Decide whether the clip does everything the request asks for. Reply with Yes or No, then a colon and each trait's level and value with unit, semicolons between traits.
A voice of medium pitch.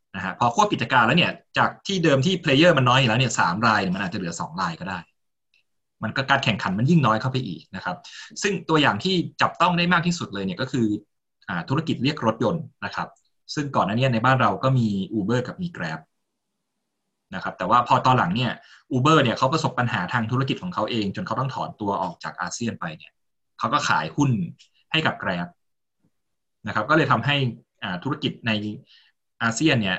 No: low, 130 Hz